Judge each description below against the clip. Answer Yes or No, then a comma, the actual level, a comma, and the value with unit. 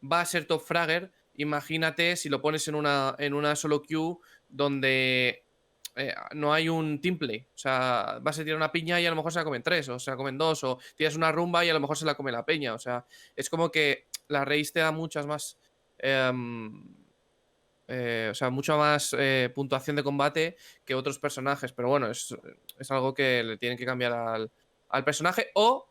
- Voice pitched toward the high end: No, medium, 145 Hz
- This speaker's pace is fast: Yes, fast, 215 wpm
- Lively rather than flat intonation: No, average, 3.3 semitones